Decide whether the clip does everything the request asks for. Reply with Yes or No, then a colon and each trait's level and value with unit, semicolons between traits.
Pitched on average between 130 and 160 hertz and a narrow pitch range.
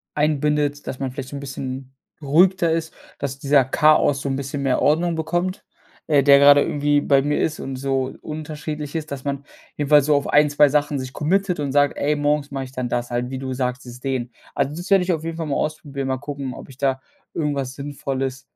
Yes: medium, 140 Hz; narrow, 2.0 semitones